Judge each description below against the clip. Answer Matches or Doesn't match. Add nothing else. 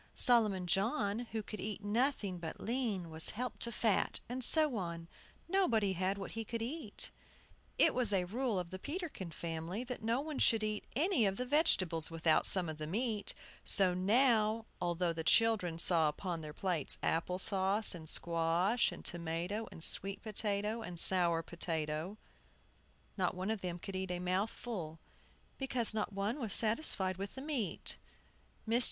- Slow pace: Doesn't match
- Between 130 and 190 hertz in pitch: Doesn't match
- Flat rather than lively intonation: Doesn't match